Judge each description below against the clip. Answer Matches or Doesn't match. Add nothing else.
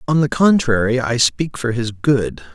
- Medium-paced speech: Matches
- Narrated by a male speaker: Matches